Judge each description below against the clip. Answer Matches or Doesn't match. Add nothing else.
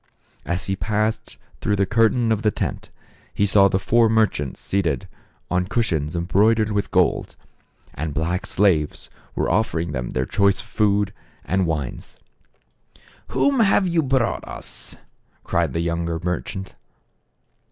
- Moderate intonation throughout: Matches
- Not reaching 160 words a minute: Matches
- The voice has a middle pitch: Doesn't match